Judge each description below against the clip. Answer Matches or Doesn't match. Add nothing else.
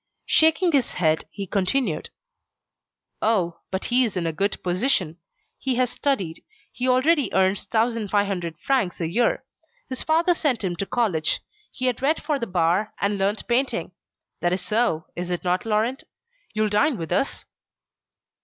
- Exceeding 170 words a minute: Doesn't match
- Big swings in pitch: Matches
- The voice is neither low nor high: Doesn't match